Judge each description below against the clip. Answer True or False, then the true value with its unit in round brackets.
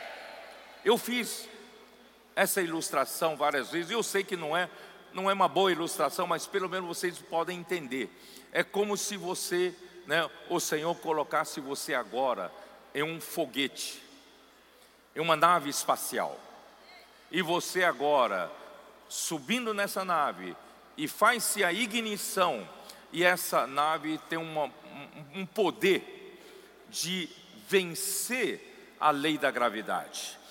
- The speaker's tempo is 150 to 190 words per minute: False (125 wpm)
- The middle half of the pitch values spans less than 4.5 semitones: True (4.0 semitones)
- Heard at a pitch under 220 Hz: True (185 Hz)